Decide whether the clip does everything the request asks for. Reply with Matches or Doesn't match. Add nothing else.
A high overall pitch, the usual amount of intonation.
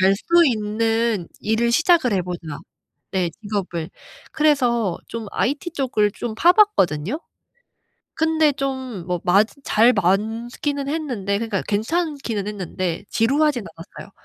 Doesn't match